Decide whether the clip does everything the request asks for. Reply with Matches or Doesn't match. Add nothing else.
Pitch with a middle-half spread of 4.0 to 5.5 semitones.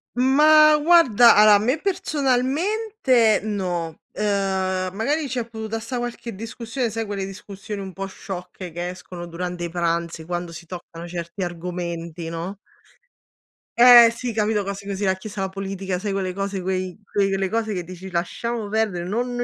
Matches